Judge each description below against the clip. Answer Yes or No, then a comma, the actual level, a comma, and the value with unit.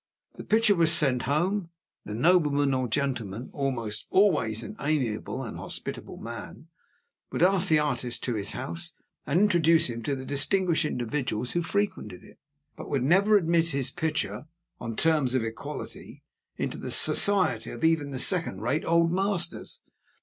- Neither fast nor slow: Yes, average, 160 wpm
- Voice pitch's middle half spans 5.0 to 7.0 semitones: Yes, wide, 5.4 semitones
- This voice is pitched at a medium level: Yes, medium, 150 Hz